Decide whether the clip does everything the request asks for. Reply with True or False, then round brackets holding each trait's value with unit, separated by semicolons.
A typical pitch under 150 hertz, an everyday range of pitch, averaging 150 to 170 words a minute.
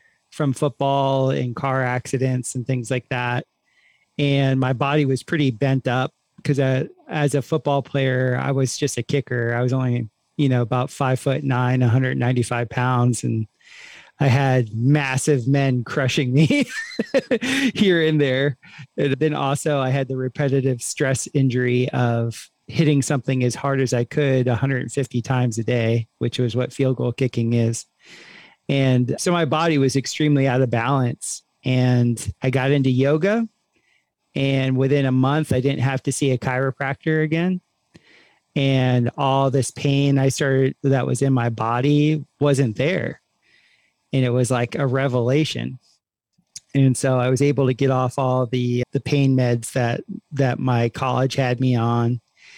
False (135 Hz; 2.2 semitones; 160 wpm)